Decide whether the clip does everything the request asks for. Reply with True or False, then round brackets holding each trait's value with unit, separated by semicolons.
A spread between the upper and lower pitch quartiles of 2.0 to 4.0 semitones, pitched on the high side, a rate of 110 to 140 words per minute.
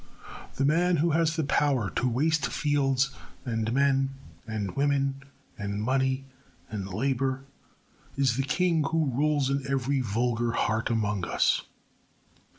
False (3.5 semitones; 135 Hz; 135 wpm)